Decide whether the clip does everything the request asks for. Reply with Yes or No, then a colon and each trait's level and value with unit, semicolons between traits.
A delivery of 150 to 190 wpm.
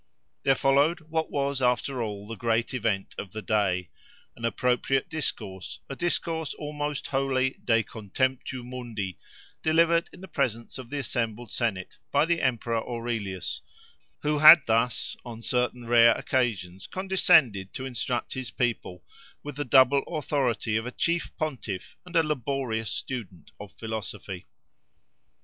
No: average, 140 wpm